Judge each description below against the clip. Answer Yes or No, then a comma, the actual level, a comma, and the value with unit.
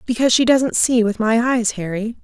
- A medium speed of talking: No, fast, 215 wpm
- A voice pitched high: Yes, high, 230 Hz